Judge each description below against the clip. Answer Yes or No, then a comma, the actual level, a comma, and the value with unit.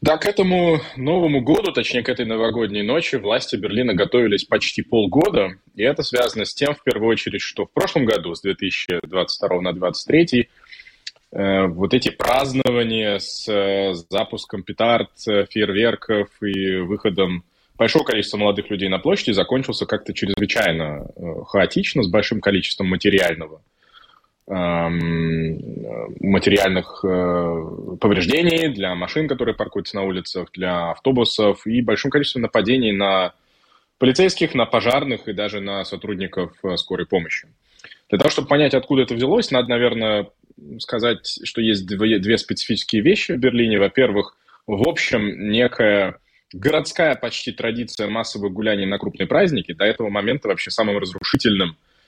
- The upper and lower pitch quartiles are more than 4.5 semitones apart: No, average, 4.1 semitones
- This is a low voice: Yes, low, 105 Hz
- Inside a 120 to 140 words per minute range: Yes, average, 130 wpm